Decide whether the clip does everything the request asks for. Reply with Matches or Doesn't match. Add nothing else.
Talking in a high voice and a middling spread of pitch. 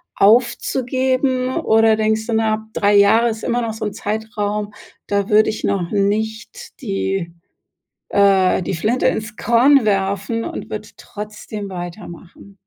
Doesn't match